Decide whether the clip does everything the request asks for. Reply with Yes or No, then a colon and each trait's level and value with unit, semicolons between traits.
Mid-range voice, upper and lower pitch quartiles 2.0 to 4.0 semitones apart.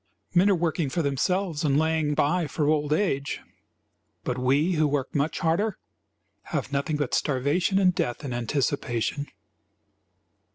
Yes: medium, 150 Hz; average, 3.4 semitones